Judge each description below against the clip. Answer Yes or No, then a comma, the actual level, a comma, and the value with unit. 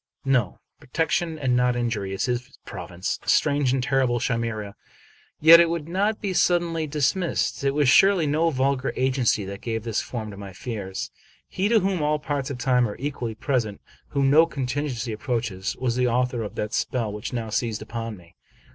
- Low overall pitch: Yes, low, 125 Hz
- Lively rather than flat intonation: No, average, 4.7 semitones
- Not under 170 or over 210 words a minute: Yes, average, 190 wpm